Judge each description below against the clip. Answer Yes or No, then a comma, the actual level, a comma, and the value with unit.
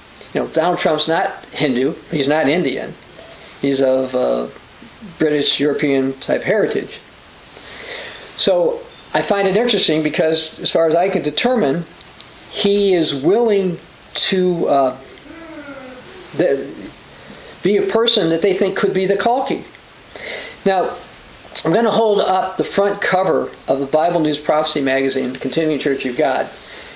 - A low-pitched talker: No, medium, 175 Hz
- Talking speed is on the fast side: No, average, 140 wpm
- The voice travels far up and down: Yes, wide, 6.7 semitones